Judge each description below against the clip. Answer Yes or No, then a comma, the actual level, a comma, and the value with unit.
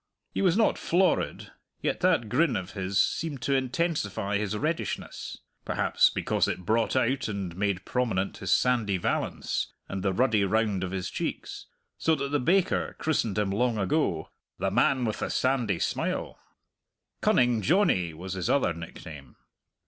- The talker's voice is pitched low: Yes, low, 110 Hz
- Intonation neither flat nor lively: No, wide, 5.8 semitones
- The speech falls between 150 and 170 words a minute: Yes, average, 155 wpm